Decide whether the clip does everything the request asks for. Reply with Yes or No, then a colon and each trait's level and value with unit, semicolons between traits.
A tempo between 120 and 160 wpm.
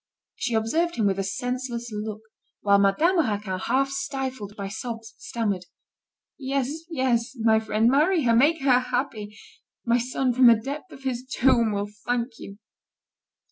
Yes: average, 155 wpm